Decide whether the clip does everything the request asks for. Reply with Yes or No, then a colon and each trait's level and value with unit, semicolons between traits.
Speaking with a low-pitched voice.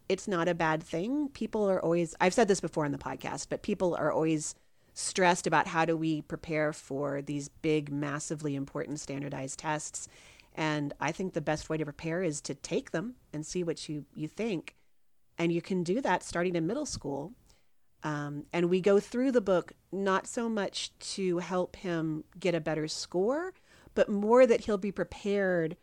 No: medium, 170 Hz